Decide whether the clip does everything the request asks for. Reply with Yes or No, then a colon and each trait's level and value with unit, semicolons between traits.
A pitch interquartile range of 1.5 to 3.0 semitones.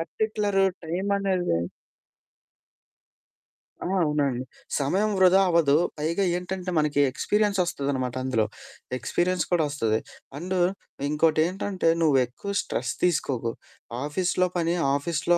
No: average, 4.5 semitones